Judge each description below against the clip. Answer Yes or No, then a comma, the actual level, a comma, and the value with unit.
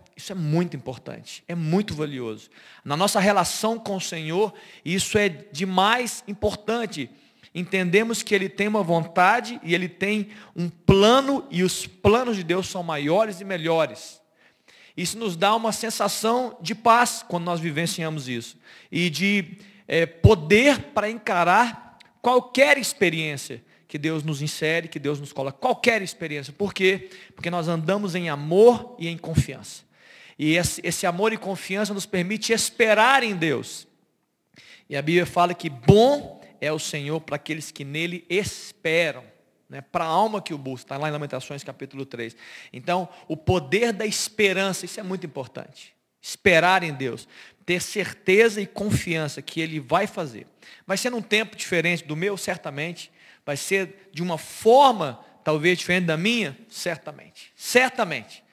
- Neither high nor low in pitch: Yes, medium, 180 Hz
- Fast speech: No, average, 155 wpm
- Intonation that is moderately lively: Yes, average, 4.9 semitones